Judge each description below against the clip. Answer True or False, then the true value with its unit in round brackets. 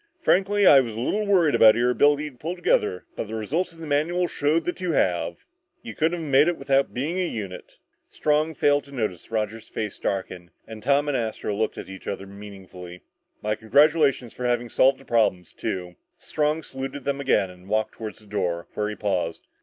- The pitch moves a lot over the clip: True (6.3 semitones)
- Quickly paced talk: True (210 wpm)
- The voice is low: True (125 Hz)